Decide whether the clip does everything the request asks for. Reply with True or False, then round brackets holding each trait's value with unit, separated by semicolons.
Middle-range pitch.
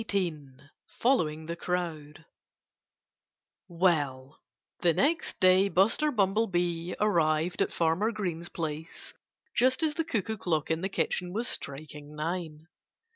True (175 Hz)